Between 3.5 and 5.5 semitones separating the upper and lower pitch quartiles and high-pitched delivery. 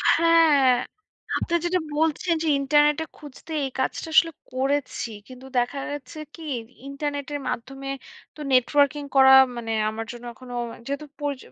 No: narrow, 2.6 semitones; very high, 285 Hz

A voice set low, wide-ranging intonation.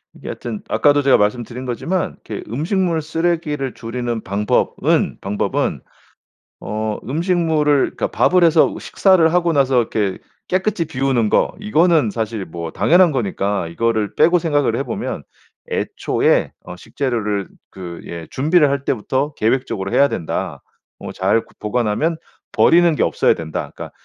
Yes: low, 130 Hz; wide, 7.3 semitones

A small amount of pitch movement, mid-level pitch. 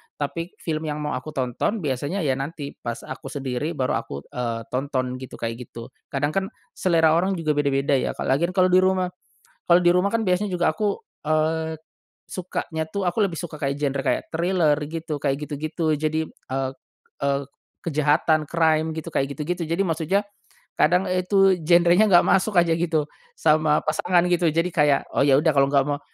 No: average, 3.7 semitones; medium, 155 Hz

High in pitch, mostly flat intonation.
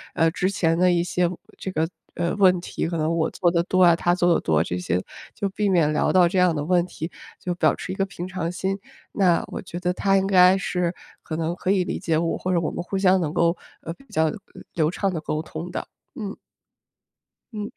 No: medium, 175 Hz; narrow, 2.1 semitones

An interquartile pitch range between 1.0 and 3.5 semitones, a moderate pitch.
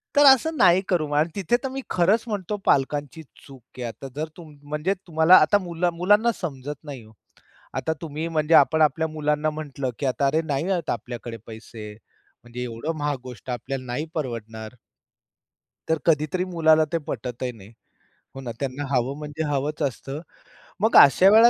No: average, 4.3 semitones; medium, 150 Hz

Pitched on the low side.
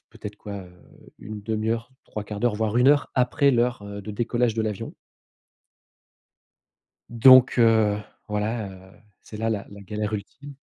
Yes: low, 110 Hz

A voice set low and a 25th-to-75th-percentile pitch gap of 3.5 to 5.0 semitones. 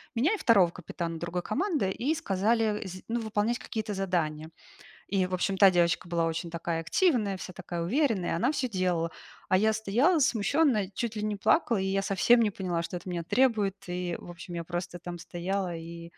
No: high, 190 Hz; average, 4.2 semitones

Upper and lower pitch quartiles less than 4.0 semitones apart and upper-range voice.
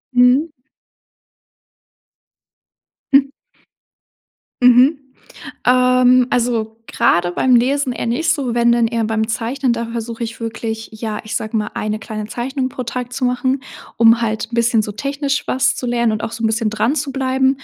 Yes: narrow, 2.5 semitones; high, 235 Hz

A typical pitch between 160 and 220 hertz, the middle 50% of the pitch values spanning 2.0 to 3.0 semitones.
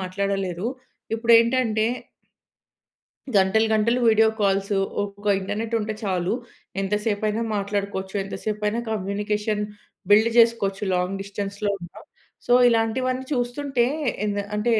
Yes: high, 210 Hz; narrow, 2.4 semitones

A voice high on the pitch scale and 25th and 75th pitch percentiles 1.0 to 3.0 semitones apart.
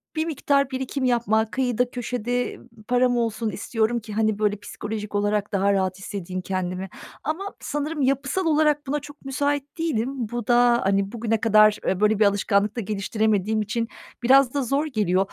No: high, 230 Hz; average, 4.4 semitones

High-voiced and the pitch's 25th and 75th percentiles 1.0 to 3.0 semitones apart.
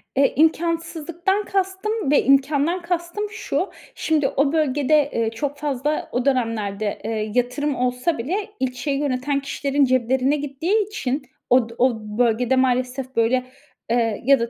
No: very high, 275 Hz; average, 4.0 semitones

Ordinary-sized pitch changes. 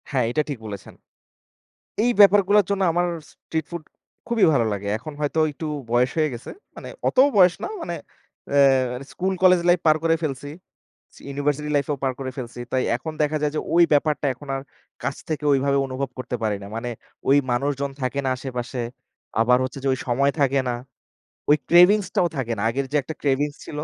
Yes: average, 3.7 semitones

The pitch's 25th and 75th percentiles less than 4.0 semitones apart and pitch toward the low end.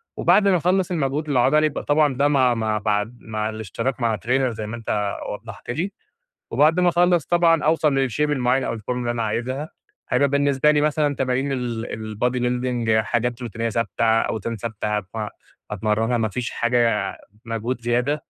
No: average, 4.4 semitones; low, 125 Hz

